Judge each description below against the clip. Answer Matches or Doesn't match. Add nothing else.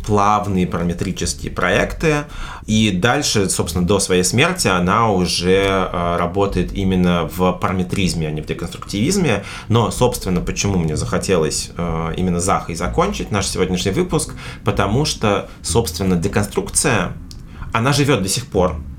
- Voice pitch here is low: Matches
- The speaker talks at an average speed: Matches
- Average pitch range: Matches